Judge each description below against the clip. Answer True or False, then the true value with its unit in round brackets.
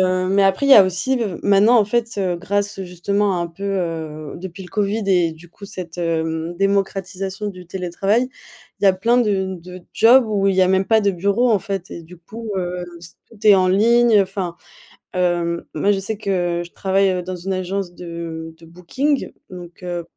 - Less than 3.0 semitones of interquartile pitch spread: True (2.5 semitones)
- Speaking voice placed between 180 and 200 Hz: True (190 Hz)